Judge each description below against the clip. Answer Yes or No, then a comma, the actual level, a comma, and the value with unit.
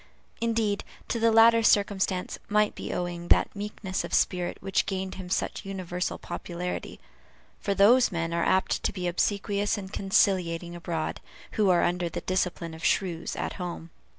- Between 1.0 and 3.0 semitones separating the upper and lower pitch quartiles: Yes, average, 2.7 semitones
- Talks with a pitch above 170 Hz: Yes, high, 190 Hz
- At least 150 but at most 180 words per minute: Yes, average, 160 wpm